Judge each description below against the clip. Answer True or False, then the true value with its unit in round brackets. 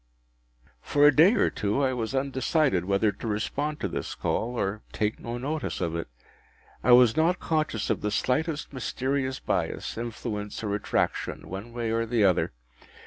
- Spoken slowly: False (165 wpm)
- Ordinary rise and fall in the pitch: True (5.0 semitones)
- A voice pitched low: True (120 Hz)